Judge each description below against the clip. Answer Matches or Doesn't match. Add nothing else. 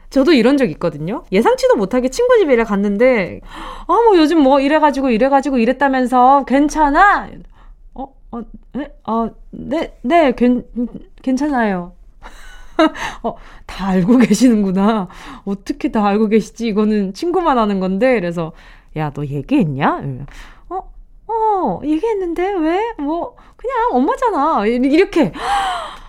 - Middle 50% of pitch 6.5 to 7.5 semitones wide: Matches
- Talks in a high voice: Matches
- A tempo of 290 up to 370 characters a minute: Doesn't match